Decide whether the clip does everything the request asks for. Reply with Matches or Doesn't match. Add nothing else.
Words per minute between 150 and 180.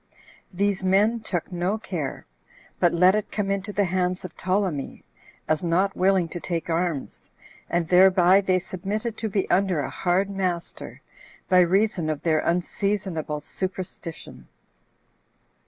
Doesn't match